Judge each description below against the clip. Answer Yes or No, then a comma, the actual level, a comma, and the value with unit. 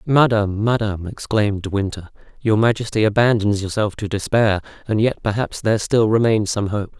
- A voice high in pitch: No, low, 105 Hz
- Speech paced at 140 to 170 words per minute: Yes, average, 165 wpm